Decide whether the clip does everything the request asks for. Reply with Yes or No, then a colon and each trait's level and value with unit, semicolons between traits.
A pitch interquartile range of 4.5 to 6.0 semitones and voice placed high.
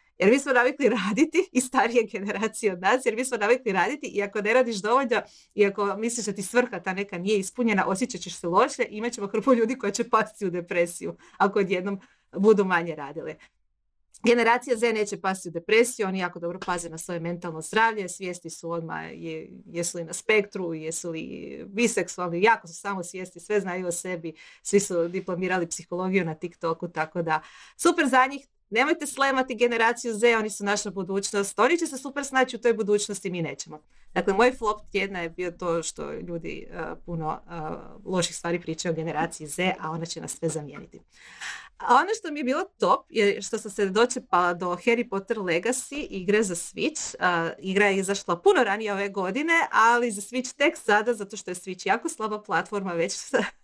Yes: average, 4.9 semitones; high, 200 Hz